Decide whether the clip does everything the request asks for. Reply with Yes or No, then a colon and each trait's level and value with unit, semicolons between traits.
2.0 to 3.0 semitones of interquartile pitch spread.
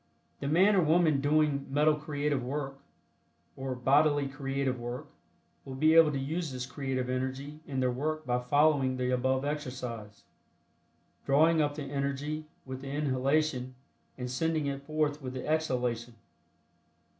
Yes: average, 2.7 semitones